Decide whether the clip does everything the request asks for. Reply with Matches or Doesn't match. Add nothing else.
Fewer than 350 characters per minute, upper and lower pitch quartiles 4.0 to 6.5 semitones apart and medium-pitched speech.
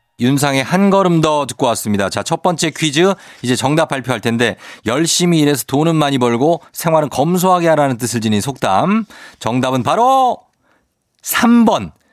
Matches